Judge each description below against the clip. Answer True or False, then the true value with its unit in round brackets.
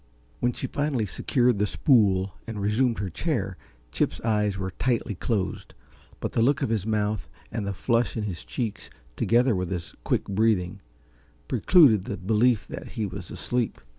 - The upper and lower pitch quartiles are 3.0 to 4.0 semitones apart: True (3.6 semitones)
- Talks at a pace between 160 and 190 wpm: True (165 wpm)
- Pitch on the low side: True (110 Hz)